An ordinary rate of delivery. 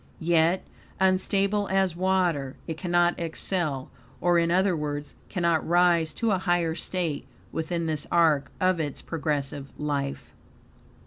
No: slow, 130 wpm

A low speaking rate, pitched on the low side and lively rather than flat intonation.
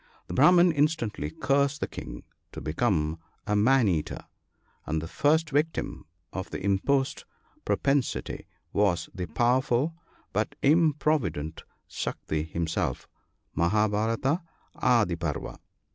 Yes: slow, 110 wpm; low, 110 Hz; wide, 8.9 semitones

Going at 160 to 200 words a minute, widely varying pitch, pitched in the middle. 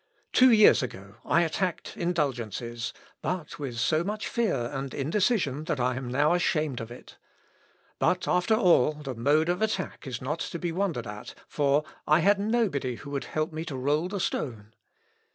Yes: average, 175 wpm; wide, 5.8 semitones; medium, 150 Hz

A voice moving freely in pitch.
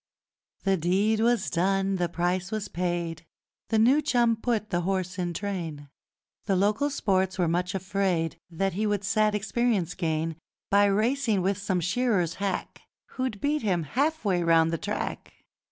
No: average, 3.6 semitones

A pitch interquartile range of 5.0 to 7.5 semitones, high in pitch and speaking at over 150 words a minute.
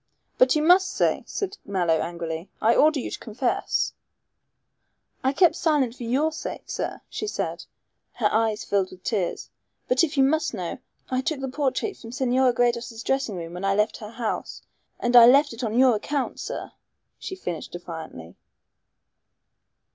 Yes: wide, 5.4 semitones; high, 245 Hz; average, 170 wpm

